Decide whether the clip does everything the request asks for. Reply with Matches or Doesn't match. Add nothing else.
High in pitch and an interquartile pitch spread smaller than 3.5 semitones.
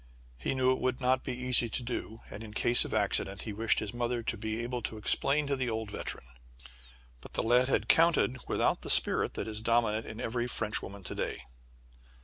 Doesn't match